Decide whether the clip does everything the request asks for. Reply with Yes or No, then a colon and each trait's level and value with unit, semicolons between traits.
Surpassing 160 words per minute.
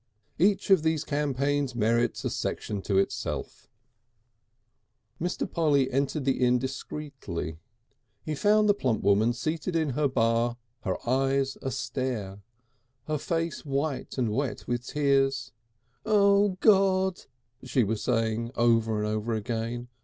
No: slow, 135 wpm